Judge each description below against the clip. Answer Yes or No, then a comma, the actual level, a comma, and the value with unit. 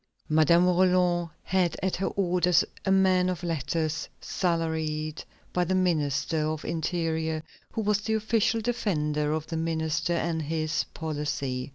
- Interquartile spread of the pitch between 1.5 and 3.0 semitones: Yes, average, 2.7 semitones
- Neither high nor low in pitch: Yes, medium, 165 Hz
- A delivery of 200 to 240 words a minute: No, average, 145 wpm